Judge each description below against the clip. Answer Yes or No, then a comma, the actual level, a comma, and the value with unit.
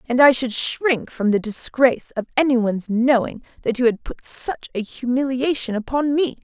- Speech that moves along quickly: No, average, 175 wpm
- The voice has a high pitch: Yes, very high, 250 Hz